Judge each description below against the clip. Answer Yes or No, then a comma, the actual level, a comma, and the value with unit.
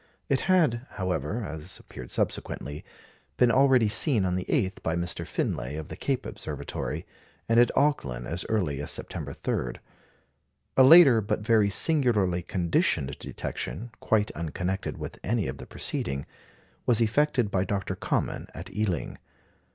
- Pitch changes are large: Yes, wide, 5.7 semitones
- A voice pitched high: No, low, 100 Hz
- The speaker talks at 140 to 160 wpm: Yes, average, 145 wpm